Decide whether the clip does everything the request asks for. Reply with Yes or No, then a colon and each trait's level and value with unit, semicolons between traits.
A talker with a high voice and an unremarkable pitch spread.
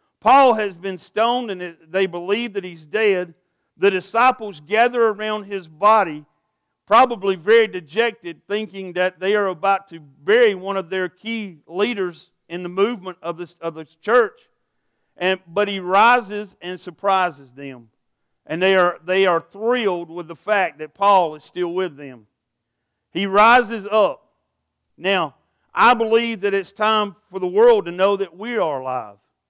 Yes: high, 195 Hz; average, 3.4 semitones